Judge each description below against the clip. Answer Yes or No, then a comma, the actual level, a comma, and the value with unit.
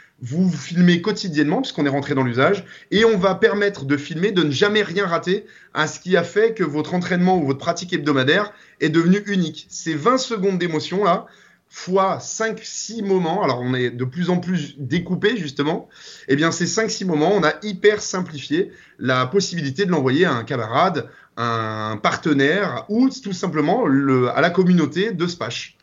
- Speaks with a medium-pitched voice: Yes, medium, 175 Hz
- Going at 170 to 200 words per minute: Yes, average, 185 wpm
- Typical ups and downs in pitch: Yes, average, 5.0 semitones